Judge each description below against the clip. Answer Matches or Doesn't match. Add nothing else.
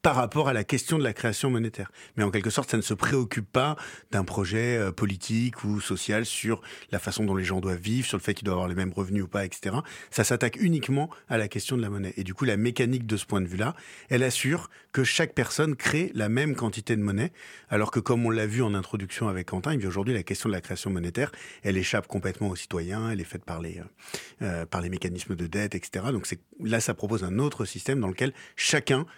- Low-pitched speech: Matches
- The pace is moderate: Doesn't match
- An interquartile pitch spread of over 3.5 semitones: Matches